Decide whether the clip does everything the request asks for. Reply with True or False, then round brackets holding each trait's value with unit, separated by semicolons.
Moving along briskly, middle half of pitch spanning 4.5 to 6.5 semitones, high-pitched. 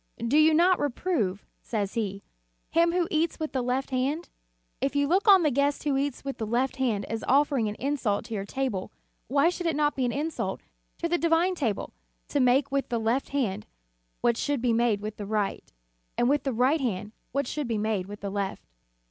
True (210 wpm; 5.1 semitones; 265 Hz)